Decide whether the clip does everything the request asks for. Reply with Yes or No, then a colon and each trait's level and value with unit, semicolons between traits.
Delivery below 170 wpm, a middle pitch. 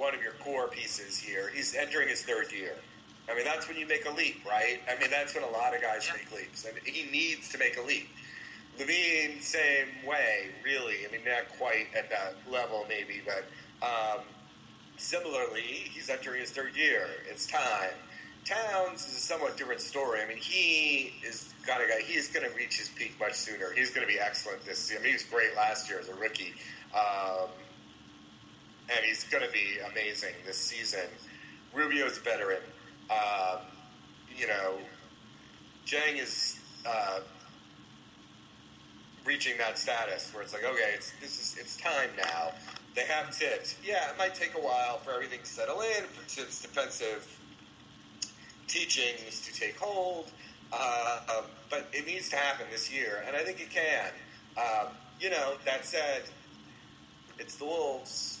No: average, 180 wpm; medium, 155 Hz